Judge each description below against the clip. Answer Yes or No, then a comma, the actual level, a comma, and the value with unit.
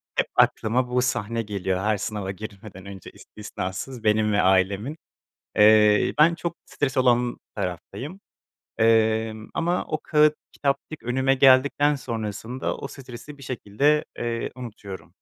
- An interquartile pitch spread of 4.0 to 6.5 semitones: Yes, average, 4.3 semitones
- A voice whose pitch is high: No, low, 115 Hz